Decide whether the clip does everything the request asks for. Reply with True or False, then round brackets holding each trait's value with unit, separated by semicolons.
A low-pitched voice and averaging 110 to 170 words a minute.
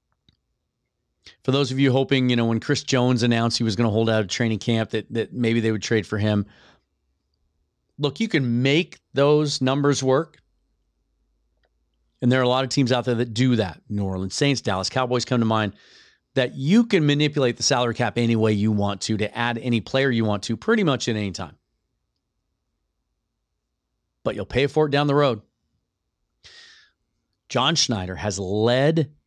False (120 Hz; 185 wpm)